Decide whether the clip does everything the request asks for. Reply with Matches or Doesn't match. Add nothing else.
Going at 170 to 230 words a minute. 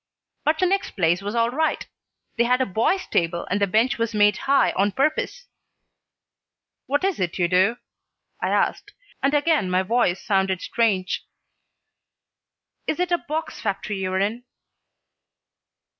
Doesn't match